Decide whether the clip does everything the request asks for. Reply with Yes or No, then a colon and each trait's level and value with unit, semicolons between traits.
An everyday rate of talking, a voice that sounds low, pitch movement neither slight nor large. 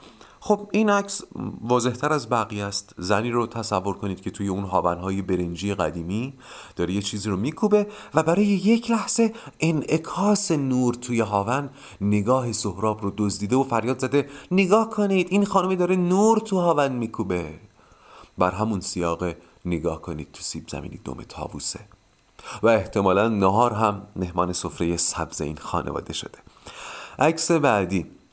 No: average, 145 wpm; low, 110 Hz; wide, 8.9 semitones